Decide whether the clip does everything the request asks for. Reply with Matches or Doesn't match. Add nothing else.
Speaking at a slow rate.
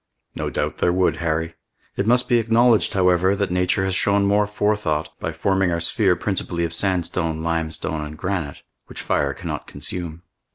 Doesn't match